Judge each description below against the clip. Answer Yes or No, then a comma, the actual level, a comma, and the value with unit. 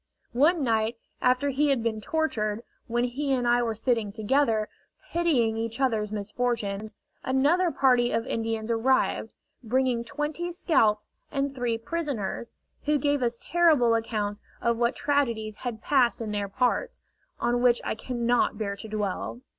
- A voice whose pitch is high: Yes, high, 240 Hz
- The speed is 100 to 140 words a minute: No, average, 150 wpm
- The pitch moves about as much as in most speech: Yes, average, 3.5 semitones